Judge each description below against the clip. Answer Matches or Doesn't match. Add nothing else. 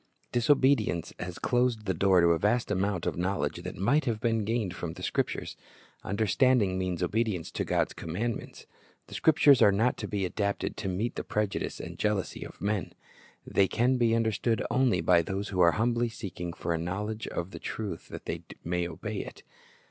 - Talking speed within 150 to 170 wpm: Doesn't match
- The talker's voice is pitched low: Matches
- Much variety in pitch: Doesn't match